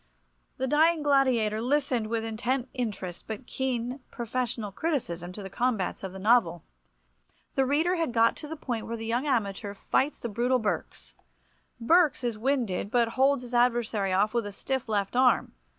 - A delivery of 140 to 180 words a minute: Yes, average, 170 wpm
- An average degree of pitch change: Yes, average, 3.7 semitones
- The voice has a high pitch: Yes, high, 235 Hz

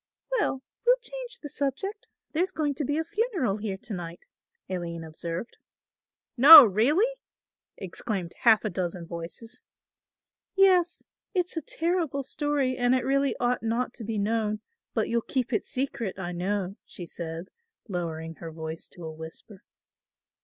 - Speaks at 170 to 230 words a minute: No, average, 150 wpm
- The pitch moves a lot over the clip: Yes, wide, 8.8 semitones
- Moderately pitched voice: No, high, 230 Hz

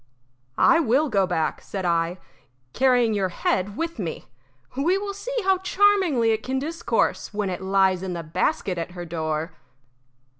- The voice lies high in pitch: Yes, high, 205 Hz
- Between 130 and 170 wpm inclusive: Yes, average, 160 wpm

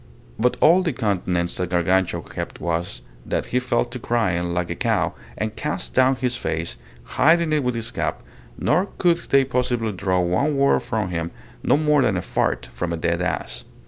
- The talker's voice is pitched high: No, low, 110 Hz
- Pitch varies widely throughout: Yes, wide, 6.9 semitones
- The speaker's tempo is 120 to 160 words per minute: No, average, 190 wpm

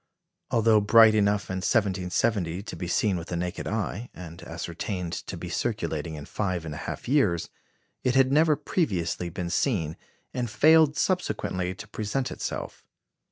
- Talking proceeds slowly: No, average, 160 wpm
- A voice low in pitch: Yes, low, 100 Hz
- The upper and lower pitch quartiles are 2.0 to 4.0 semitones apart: No, average, 5.2 semitones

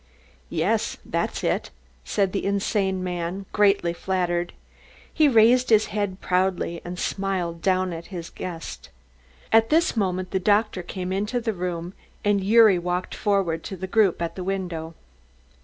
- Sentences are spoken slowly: No, average, 150 wpm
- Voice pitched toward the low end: No, high, 190 Hz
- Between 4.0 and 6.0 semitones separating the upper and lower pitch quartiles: No, average, 2.7 semitones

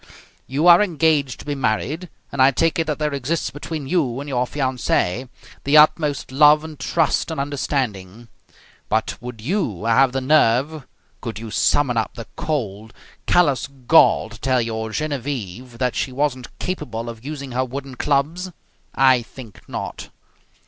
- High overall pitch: No, low, 135 Hz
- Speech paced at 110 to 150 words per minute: No, average, 160 wpm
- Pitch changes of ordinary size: Yes, average, 4.0 semitones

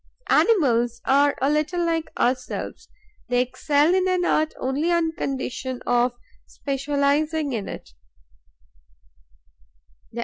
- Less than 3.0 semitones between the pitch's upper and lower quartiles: No, average, 4.1 semitones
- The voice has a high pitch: Yes, very high, 285 Hz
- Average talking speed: No, slow, 105 wpm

